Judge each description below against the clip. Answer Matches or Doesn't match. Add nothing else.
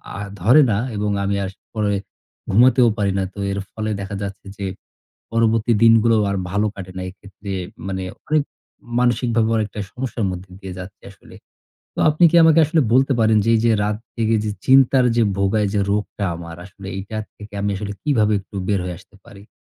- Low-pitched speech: Matches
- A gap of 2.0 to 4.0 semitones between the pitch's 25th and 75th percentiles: Matches